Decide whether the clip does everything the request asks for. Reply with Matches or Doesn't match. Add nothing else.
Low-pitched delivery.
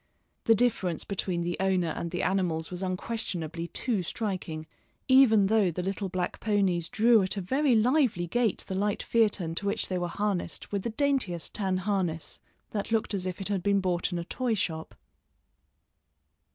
Doesn't match